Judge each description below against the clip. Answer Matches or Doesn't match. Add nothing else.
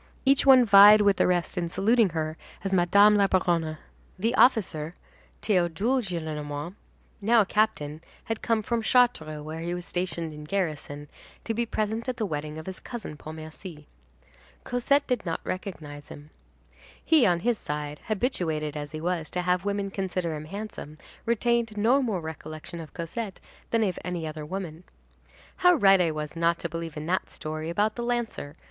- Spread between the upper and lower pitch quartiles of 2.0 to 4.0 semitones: Doesn't match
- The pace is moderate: Matches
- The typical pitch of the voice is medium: Matches